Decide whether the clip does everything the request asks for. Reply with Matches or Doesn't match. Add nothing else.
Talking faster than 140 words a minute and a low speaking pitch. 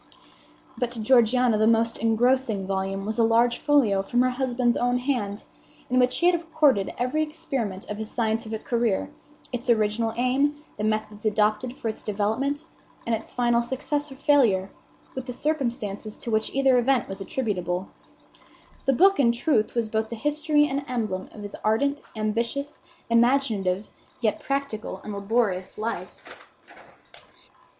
Doesn't match